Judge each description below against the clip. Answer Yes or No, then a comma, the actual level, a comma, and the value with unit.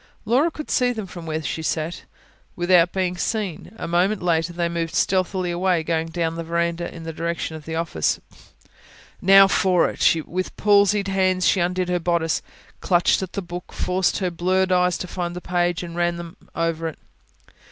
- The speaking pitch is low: No, medium, 175 Hz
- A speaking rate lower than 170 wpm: No, average, 185 wpm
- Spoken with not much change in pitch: Yes, narrow, 2.0 semitones